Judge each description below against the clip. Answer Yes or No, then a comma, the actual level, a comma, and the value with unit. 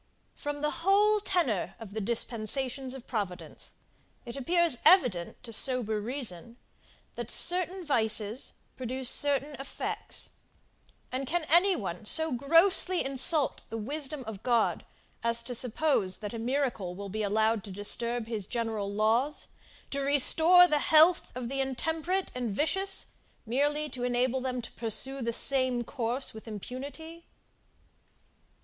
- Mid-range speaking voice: No, very high, 255 Hz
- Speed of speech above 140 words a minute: No, slow, 135 wpm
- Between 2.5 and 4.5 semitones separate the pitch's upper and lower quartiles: No, average, 5.0 semitones